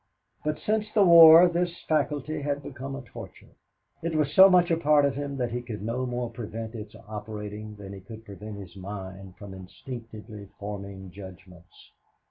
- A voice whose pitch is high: No, low, 115 Hz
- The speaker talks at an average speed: Yes, average, 175 wpm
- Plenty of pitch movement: Yes, wide, 6.4 semitones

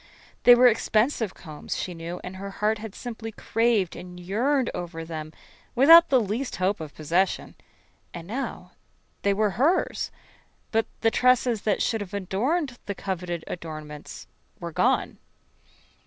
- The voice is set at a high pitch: Yes, high, 205 Hz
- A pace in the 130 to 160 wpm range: Yes, average, 145 wpm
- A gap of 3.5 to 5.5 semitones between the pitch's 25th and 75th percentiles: Yes, average, 5.1 semitones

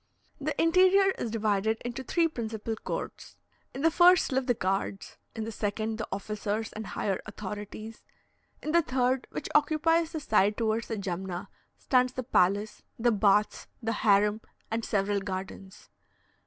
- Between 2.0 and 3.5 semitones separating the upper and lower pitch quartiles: No, average, 4.3 semitones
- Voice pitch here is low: No, high, 220 Hz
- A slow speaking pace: No, average, 155 wpm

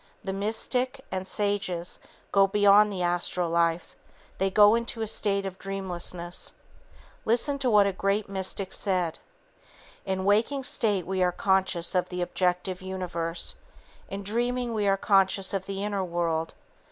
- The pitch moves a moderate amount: No, narrow, 2.3 semitones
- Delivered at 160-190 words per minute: No, average, 150 wpm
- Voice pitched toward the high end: Yes, high, 195 Hz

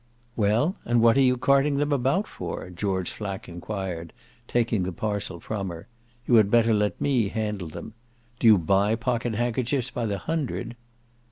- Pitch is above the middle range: No, low, 110 Hz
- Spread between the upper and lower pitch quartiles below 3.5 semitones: No, average, 3.8 semitones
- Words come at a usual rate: Yes, average, 165 wpm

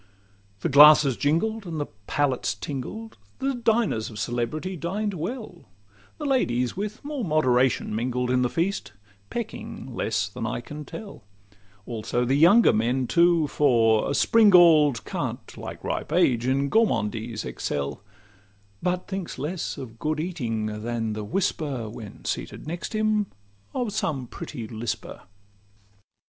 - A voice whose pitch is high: No, medium, 145 Hz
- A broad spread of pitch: Yes, wide, 7.8 semitones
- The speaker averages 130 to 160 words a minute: Yes, slow, 135 wpm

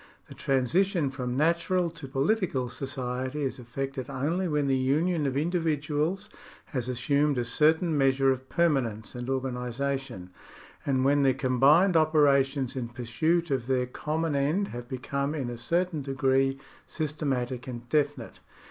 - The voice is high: No, low, 135 Hz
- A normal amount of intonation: Yes, average, 3.2 semitones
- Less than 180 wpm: Yes, average, 150 wpm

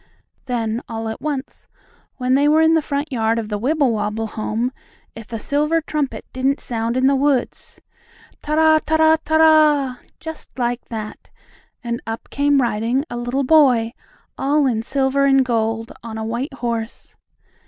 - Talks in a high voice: Yes, very high, 255 Hz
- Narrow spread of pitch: No, average, 4.2 semitones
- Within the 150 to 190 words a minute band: Yes, average, 165 wpm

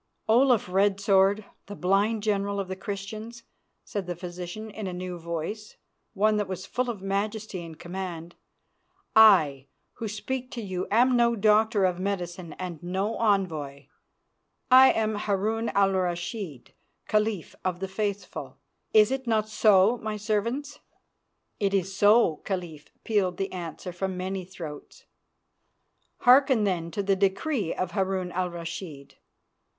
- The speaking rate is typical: Yes, average, 145 wpm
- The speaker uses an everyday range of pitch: Yes, average, 3.1 semitones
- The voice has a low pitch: No, high, 195 Hz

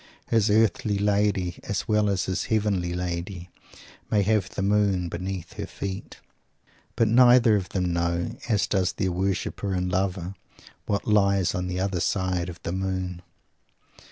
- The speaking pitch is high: No, very low, 95 Hz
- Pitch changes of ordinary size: No, narrow, 2.3 semitones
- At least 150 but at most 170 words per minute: Yes, average, 155 wpm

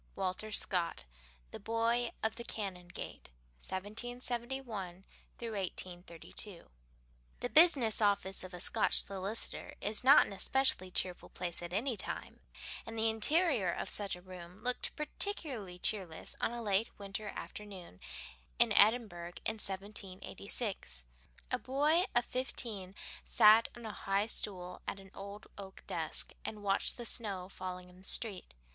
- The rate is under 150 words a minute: Yes, average, 140 wpm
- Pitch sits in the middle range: No, high, 205 Hz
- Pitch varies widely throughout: No, average, 3.8 semitones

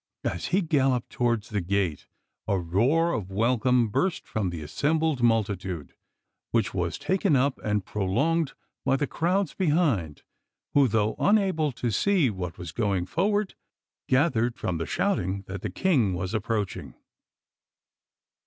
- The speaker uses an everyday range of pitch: No, wide, 8.3 semitones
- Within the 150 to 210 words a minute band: No, average, 140 wpm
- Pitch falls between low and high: No, low, 115 Hz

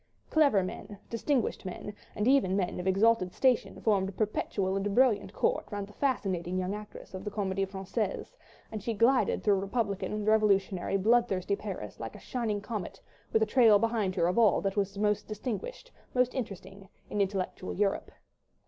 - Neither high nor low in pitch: No, high, 205 Hz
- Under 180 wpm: Yes, average, 170 wpm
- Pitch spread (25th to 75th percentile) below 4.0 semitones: Yes, average, 2.9 semitones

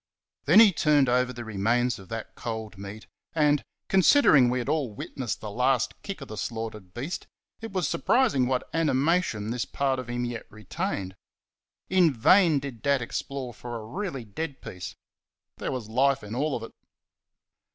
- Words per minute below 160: No, average, 170 wpm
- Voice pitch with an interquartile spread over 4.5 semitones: Yes, average, 4.9 semitones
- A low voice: Yes, low, 125 Hz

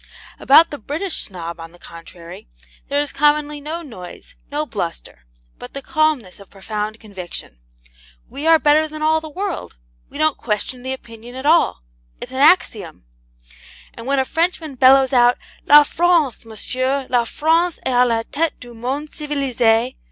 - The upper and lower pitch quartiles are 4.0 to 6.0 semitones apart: Yes, average, 5.3 semitones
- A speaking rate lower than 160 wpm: No, average, 165 wpm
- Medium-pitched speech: No, very high, 265 Hz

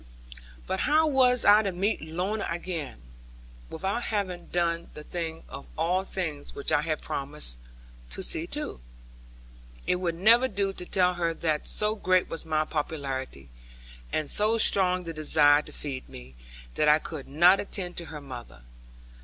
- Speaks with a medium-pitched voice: Yes, medium, 170 Hz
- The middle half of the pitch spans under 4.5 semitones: Yes, average, 4.1 semitones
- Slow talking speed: No, average, 160 wpm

